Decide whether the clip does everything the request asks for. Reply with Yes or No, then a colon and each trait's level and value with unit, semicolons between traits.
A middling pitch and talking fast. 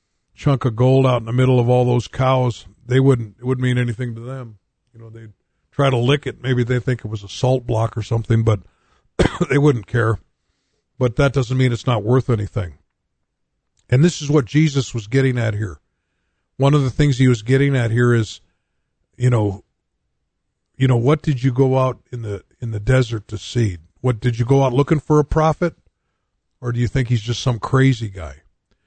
No: low, 125 Hz; fast, 210 wpm